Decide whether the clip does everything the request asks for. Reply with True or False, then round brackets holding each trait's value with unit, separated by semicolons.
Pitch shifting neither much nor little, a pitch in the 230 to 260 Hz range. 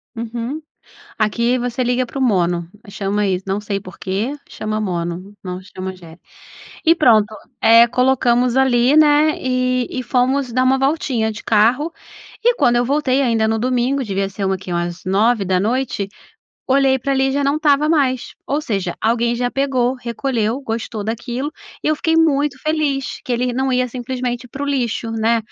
True (3.9 semitones; 245 Hz)